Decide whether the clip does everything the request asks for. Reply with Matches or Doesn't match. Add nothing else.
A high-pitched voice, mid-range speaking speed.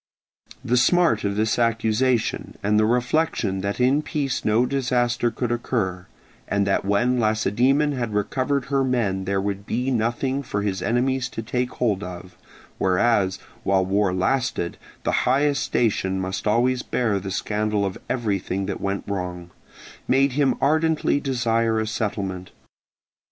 Doesn't match